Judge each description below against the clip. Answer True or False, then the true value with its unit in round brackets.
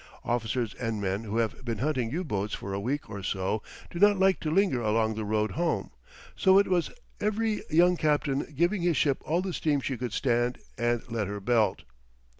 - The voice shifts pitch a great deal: True (7.7 semitones)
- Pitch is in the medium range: False (125 Hz)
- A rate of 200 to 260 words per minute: True (205 wpm)